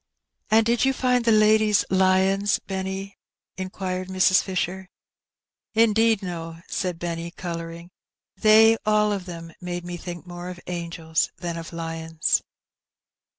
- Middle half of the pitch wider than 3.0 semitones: Yes, average, 3.6 semitones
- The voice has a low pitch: No, medium, 185 Hz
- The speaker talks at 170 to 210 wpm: No, average, 145 wpm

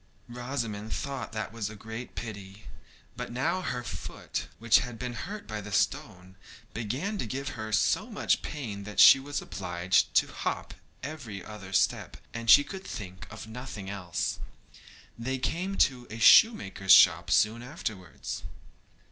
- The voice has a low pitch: Yes, low, 110 Hz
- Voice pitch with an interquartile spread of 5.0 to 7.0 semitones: No, average, 4.6 semitones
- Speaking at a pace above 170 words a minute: No, average, 155 wpm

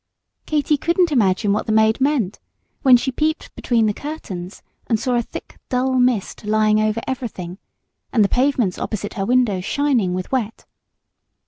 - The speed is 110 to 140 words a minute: No, average, 160 wpm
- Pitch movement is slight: No, average, 4.1 semitones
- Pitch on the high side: Yes, high, 230 Hz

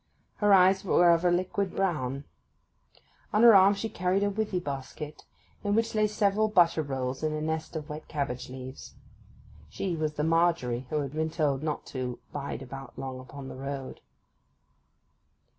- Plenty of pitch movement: Yes, wide, 5.7 semitones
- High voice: No, medium, 155 Hz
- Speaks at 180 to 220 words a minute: No, average, 170 wpm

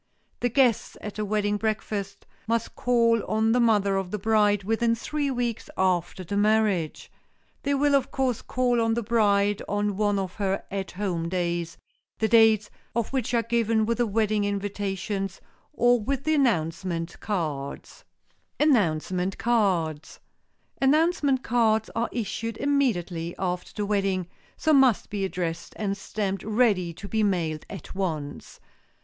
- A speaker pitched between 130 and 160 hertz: No, high, 210 Hz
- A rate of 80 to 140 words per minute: No, average, 150 wpm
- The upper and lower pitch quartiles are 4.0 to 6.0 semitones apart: No, average, 3.6 semitones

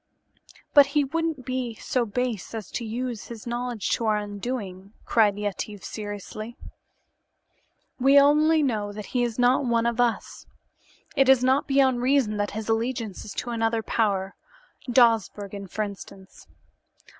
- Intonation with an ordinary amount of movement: Yes, average, 3.6 semitones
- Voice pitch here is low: No, high, 230 Hz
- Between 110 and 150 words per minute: Yes, average, 145 wpm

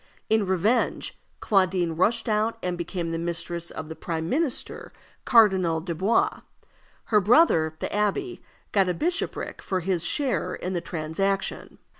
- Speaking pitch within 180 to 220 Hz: Yes, high, 190 Hz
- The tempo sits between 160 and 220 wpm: No, average, 140 wpm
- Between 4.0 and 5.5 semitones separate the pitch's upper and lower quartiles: Yes, average, 4.5 semitones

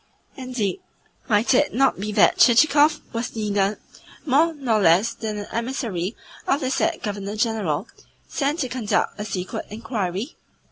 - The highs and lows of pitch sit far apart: No, average, 4.5 semitones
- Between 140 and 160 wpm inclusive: Yes, average, 145 wpm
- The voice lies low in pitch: No, high, 230 Hz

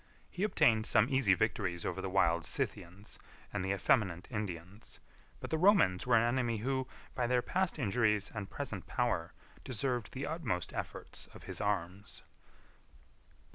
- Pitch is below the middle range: Yes, low, 110 Hz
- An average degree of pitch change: Yes, average, 5.0 semitones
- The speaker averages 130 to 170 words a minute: Yes, average, 150 wpm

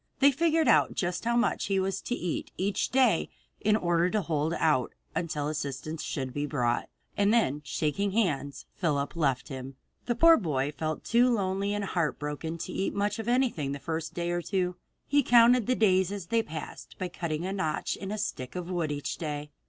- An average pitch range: No, wide, 5.7 semitones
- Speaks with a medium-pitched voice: Yes, medium, 175 Hz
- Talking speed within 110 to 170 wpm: No, average, 200 wpm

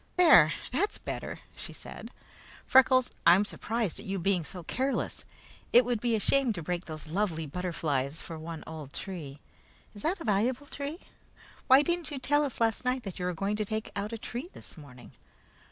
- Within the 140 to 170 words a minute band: No, average, 185 wpm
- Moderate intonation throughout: No, wide, 7.5 semitones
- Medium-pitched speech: No, high, 210 Hz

